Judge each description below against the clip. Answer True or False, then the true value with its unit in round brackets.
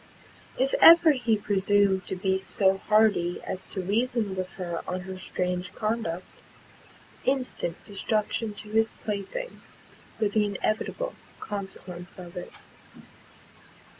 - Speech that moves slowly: True (120 wpm)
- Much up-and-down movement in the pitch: False (3.1 semitones)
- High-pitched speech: True (200 Hz)